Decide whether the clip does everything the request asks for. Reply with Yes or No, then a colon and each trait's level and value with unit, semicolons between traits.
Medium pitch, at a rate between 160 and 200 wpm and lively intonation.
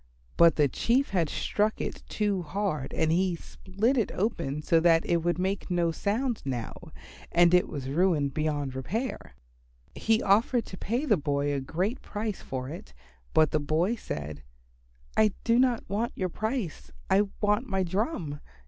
Yes: medium, 180 Hz; average, 165 wpm; wide, 5.7 semitones